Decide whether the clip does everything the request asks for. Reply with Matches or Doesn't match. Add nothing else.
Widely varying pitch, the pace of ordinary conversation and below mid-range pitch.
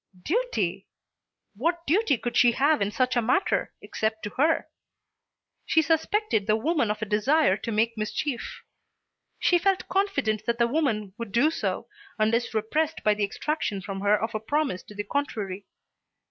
Doesn't match